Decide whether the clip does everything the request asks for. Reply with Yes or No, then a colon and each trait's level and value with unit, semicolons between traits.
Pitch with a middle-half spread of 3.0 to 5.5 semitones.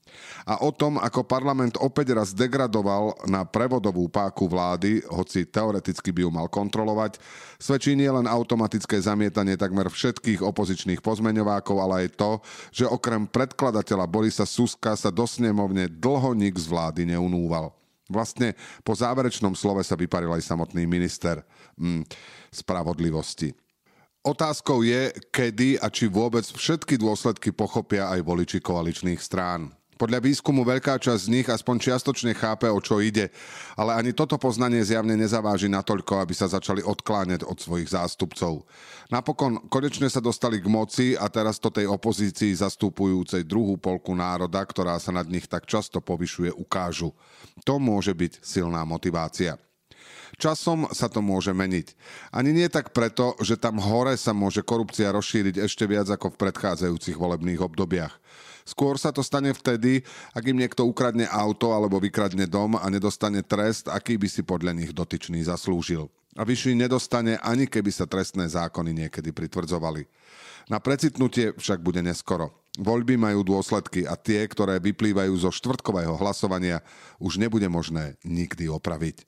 Yes: average, 4.6 semitones